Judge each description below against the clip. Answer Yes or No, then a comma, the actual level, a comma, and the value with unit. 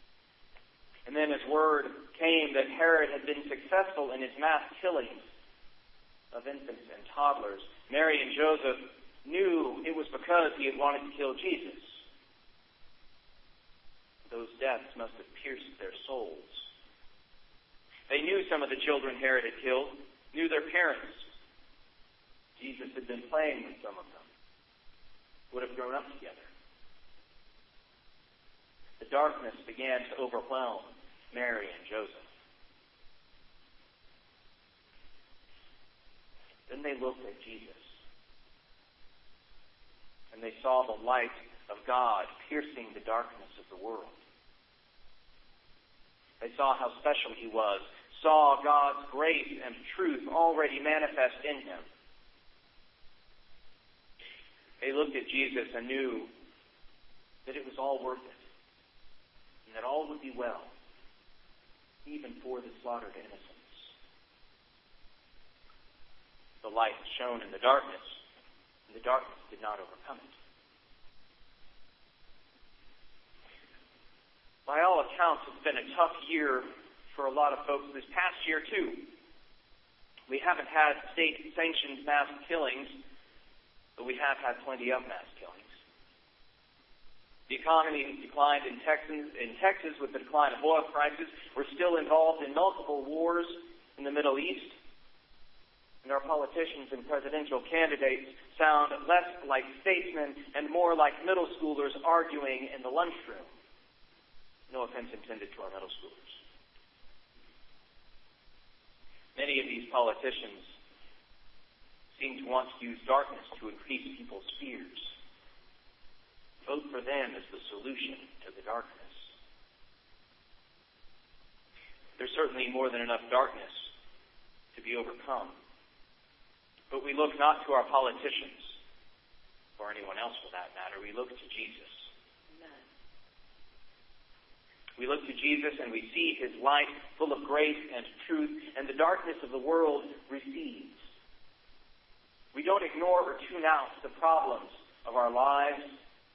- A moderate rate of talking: No, slow, 125 wpm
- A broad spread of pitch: No, average, 3.7 semitones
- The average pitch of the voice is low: No, medium, 145 Hz